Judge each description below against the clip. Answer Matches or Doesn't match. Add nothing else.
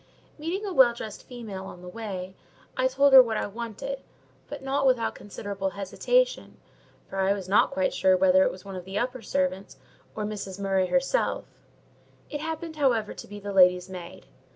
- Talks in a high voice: Matches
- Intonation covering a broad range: Matches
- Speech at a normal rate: Matches